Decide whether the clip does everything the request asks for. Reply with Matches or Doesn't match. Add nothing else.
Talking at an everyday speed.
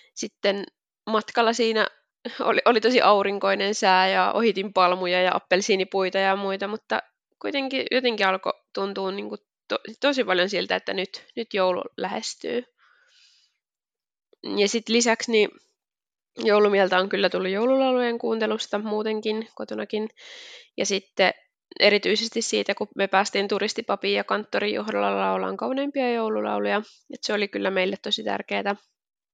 Matches